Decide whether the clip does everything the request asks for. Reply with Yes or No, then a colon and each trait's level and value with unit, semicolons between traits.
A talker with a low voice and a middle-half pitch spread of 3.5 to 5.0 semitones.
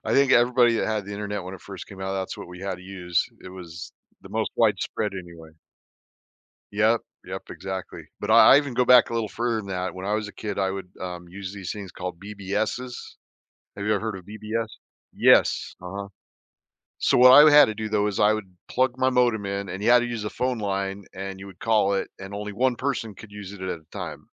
No: low, 105 Hz; average, 3.0 semitones